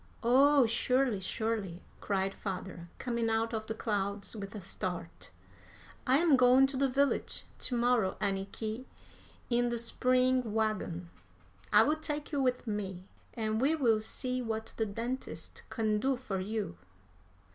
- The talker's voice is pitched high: Yes, high, 225 Hz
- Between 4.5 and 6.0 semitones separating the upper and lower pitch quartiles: No, average, 3.9 semitones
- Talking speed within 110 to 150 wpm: Yes, average, 145 wpm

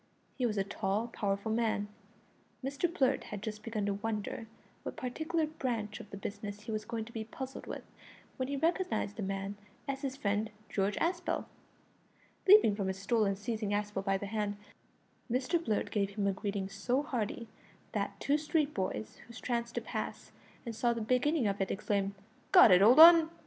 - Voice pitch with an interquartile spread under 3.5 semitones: No, average, 4.3 semitones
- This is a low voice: No, high, 220 Hz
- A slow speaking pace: No, average, 185 wpm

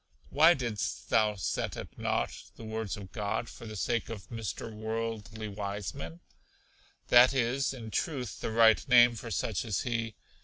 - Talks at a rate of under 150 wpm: No, average, 160 wpm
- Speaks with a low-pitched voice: Yes, low, 110 Hz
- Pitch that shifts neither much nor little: No, narrow, 2.1 semitones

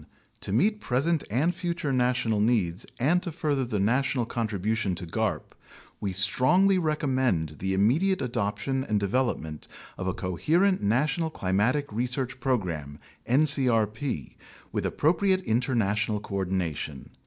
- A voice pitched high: No, low, 120 Hz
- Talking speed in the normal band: No, slow, 120 wpm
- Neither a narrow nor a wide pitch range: No, wide, 6.7 semitones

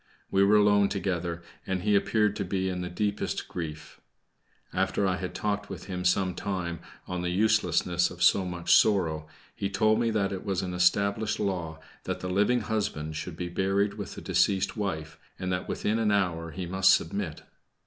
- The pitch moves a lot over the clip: No, narrow, 2.5 semitones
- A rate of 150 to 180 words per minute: No, average, 190 wpm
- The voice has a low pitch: Yes, very low, 95 Hz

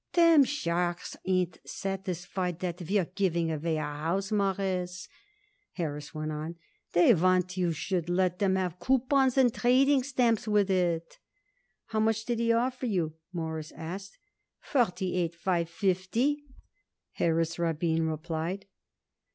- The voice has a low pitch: No, medium, 185 Hz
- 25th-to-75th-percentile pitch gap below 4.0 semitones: No, average, 4.4 semitones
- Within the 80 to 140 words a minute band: Yes, slow, 135 wpm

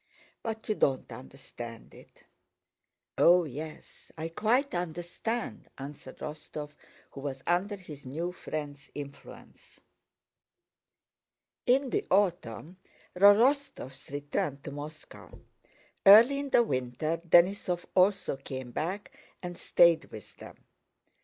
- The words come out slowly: Yes, slow, 110 wpm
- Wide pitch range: Yes, wide, 6.0 semitones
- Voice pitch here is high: No, medium, 165 Hz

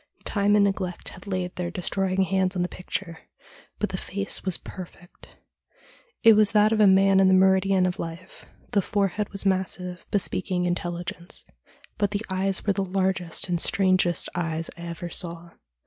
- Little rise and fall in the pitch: Yes, narrow, 1.8 semitones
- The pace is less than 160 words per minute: No, average, 170 wpm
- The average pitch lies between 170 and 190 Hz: Yes, medium, 185 Hz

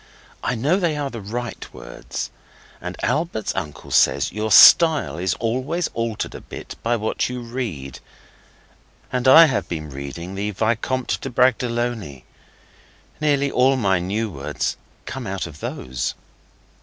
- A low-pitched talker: Yes, low, 115 Hz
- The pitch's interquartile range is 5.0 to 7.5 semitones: Yes, wide, 5.6 semitones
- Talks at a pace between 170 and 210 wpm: No, average, 145 wpm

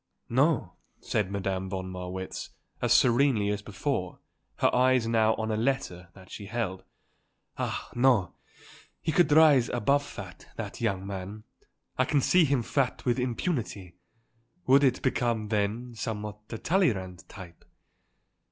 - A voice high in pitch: No, low, 110 Hz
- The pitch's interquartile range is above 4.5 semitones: Yes, average, 5.0 semitones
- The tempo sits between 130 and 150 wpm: Yes, average, 140 wpm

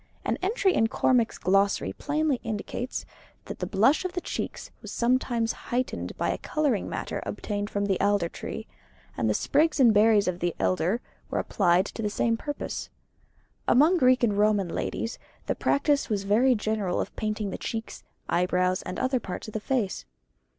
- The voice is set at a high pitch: Yes, high, 220 Hz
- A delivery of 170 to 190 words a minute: Yes, average, 175 wpm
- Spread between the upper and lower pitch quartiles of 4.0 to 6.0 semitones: Yes, average, 4.5 semitones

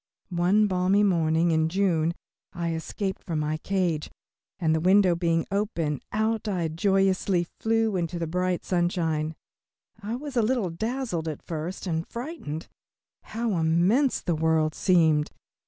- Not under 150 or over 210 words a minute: No, average, 140 wpm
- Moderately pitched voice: Yes, medium, 175 Hz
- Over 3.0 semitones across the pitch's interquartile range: Yes, average, 4.0 semitones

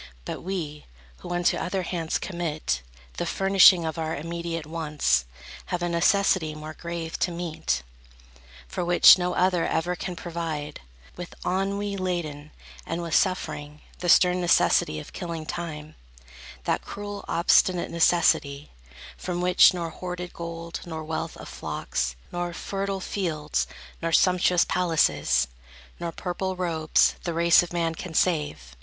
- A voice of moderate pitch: Yes, medium, 170 Hz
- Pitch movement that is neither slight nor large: No, narrow, 2.2 semitones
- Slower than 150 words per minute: Yes, average, 140 wpm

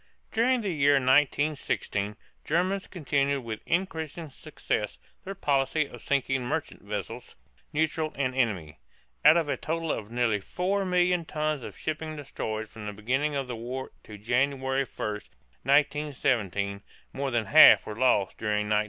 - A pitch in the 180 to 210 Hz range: No, medium, 140 Hz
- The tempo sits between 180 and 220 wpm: No, average, 145 wpm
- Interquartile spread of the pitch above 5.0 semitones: Yes, wide, 5.6 semitones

